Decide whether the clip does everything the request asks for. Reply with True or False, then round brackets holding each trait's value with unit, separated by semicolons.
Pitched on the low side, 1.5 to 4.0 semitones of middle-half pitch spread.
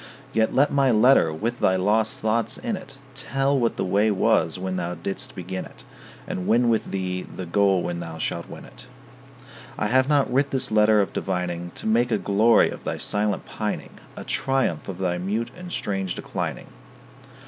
False (105 Hz; 4.8 semitones)